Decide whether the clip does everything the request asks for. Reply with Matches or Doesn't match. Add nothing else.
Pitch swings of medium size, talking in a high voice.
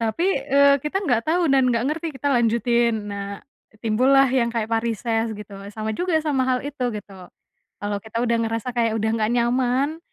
Matches